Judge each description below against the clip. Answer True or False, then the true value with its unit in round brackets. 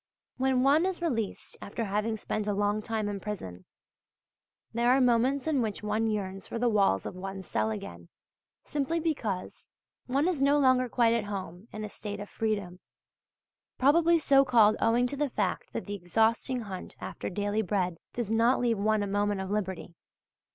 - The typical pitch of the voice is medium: False (215 Hz)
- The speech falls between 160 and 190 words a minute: True (180 wpm)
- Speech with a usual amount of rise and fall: True (4.1 semitones)